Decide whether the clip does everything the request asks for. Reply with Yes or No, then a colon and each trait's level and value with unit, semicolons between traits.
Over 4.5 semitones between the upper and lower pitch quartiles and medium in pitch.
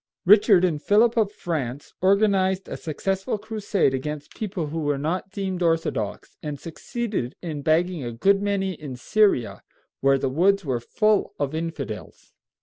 Yes: wide, 5.4 semitones; medium, 175 Hz